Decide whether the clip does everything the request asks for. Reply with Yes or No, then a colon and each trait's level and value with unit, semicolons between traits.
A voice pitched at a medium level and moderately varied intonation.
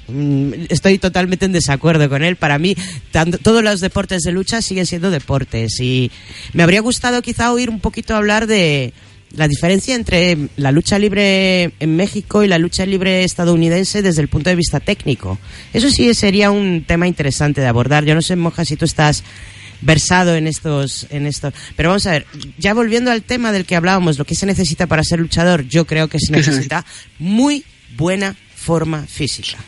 Yes: medium, 170 Hz; average, 4.9 semitones